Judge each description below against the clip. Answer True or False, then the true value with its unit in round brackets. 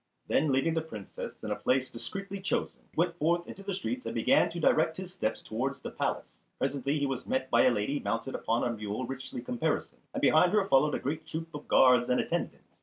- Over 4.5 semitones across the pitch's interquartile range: True (5.2 semitones)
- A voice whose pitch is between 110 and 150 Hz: True (140 Hz)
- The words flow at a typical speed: False (225 wpm)